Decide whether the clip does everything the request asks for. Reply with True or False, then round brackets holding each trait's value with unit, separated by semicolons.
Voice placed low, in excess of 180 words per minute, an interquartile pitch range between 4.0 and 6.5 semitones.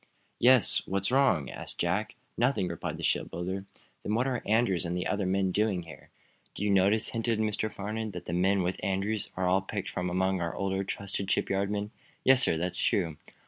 False (100 Hz; 195 wpm; 2.7 semitones)